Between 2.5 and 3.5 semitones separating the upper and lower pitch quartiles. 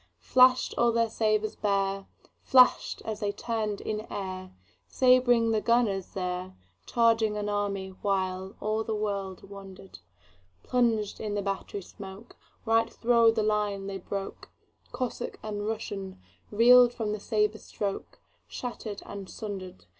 Yes: average, 2.8 semitones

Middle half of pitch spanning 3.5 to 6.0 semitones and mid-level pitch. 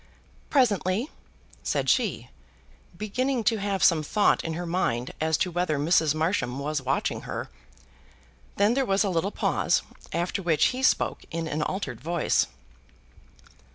Yes: average, 4.6 semitones; medium, 175 Hz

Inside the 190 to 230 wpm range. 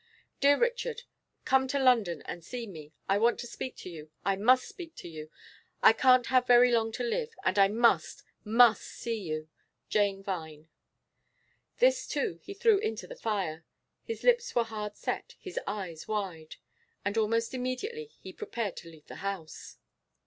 No: average, 170 wpm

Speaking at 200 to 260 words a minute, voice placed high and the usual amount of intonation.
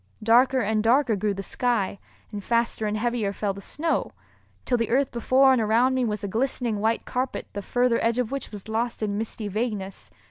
Yes: fast, 205 wpm; high, 230 Hz; average, 3.0 semitones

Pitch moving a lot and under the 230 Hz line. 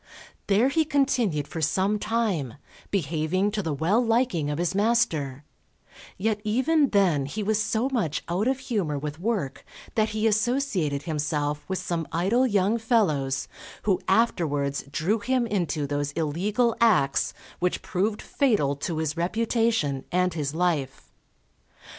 Yes: wide, 6.9 semitones; medium, 185 Hz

